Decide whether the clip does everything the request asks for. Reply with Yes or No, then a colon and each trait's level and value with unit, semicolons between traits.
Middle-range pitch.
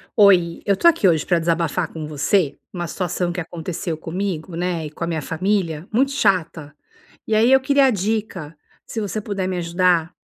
Yes: medium, 180 Hz